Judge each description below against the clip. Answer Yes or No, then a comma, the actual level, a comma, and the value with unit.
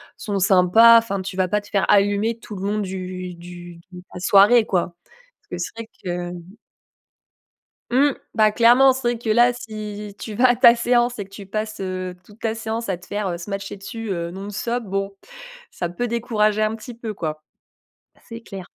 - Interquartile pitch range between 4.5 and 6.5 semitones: No, average, 3.6 semitones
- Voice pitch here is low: No, high, 205 Hz